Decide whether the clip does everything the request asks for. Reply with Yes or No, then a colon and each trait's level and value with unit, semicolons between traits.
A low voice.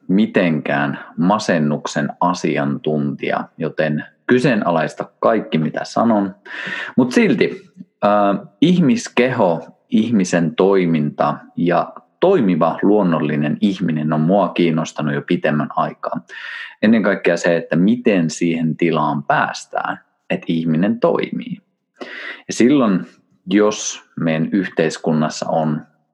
Yes: very low, 80 Hz